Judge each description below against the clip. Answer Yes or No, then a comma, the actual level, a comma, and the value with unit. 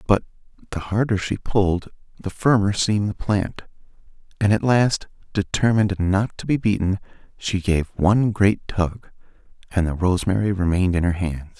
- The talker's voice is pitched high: No, low, 100 Hz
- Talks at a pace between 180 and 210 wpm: No, average, 155 wpm